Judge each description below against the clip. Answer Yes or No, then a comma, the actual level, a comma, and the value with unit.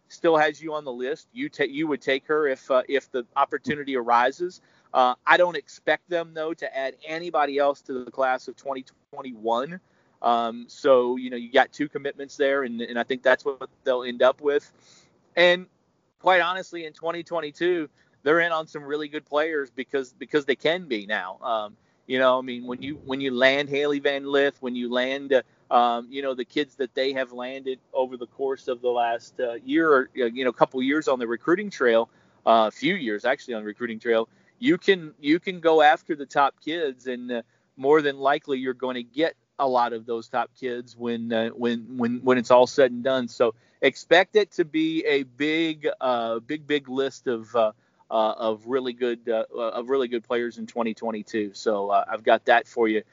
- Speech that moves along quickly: Yes, fast, 210 wpm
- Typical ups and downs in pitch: Yes, average, 4.0 semitones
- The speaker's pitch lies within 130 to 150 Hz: Yes, low, 135 Hz